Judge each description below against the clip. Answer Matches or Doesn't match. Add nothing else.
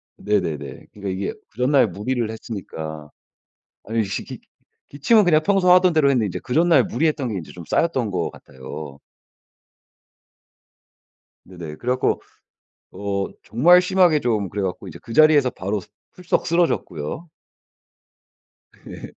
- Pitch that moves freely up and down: Matches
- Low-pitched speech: Matches